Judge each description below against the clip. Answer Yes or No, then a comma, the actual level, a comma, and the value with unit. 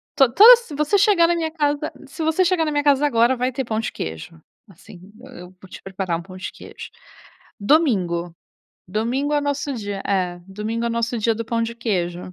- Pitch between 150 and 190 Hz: No, high, 235 Hz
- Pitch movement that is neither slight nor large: No, wide, 7.2 semitones